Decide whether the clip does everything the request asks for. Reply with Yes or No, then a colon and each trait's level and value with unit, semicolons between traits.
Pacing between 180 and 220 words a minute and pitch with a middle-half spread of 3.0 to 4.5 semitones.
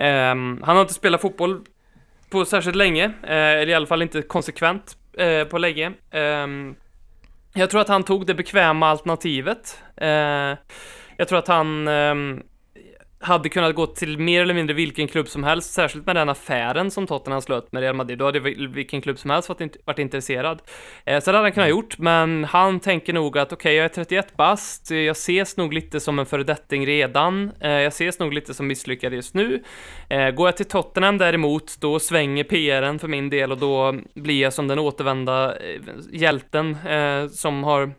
Yes: average, 190 wpm; average, 3.9 semitones